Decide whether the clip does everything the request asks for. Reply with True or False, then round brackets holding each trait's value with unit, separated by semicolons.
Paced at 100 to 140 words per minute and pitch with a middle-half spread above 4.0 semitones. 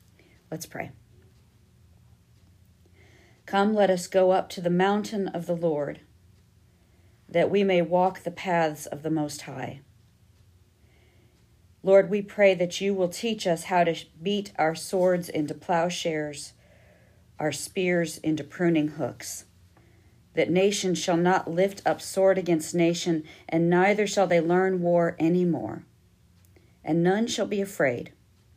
True (135 wpm; 5.5 semitones)